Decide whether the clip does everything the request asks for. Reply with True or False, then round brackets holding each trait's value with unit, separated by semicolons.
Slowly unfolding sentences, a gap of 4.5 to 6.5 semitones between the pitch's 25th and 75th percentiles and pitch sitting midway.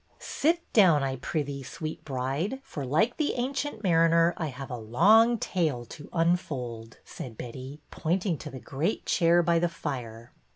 False (160 wpm; 5.5 semitones; 155 Hz)